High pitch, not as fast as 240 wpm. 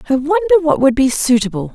Yes: very high, 255 Hz; fast, 205 wpm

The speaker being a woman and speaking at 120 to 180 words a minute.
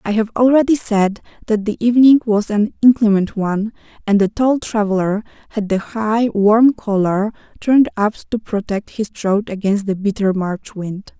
Yes: female; average, 165 wpm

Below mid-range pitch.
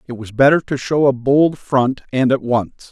Yes: low, 130 Hz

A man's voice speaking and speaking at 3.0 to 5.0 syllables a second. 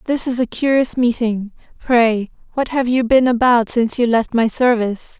No: female; 4.9 syllables/s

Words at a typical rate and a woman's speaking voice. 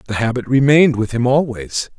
No: average, 180 wpm; male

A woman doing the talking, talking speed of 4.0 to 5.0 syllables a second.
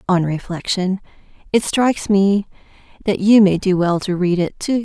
Yes: female; 4.8 syllables/s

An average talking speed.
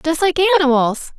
Yes: average, 150 wpm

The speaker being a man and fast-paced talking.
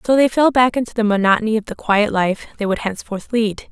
No: female; fast, 240 wpm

